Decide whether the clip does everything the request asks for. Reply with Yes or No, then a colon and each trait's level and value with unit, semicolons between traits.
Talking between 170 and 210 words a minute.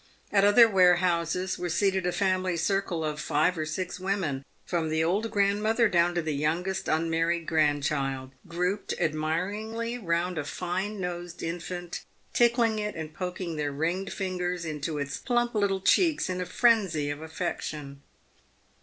No: average, 155 wpm